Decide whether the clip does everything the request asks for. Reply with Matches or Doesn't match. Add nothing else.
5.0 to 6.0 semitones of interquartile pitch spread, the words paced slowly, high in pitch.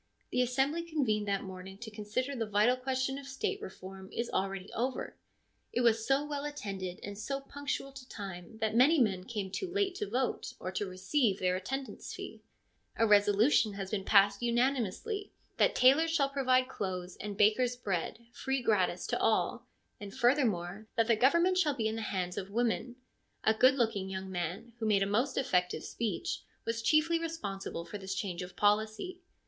Doesn't match